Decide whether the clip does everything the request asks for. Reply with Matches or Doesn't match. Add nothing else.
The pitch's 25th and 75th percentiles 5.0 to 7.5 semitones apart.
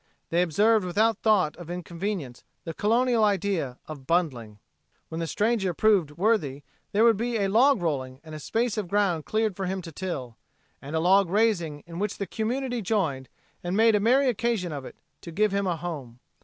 Matches